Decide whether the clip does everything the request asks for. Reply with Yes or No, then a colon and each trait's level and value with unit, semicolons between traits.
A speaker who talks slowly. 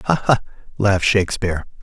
Yes: slow, 130 wpm